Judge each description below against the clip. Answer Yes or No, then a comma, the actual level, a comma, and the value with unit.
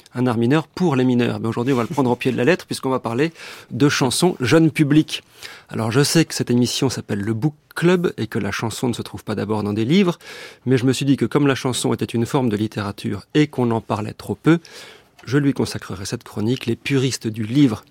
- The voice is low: Yes, low, 125 Hz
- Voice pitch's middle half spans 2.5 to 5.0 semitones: Yes, average, 4.3 semitones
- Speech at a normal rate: No, fast, 250 wpm